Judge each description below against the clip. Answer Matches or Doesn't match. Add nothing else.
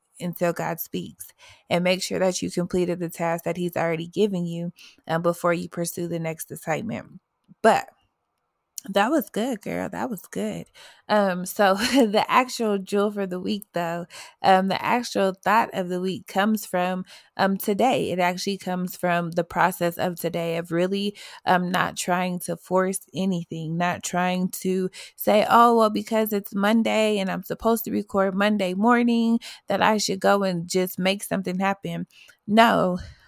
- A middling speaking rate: Matches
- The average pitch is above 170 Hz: Matches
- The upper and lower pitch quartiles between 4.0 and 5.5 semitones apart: Doesn't match